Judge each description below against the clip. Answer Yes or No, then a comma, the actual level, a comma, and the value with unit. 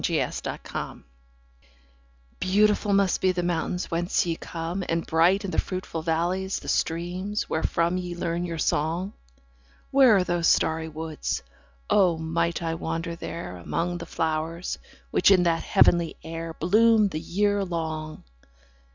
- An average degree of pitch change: No, narrow, 2.2 semitones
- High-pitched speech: No, medium, 170 Hz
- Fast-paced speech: No, average, 145 wpm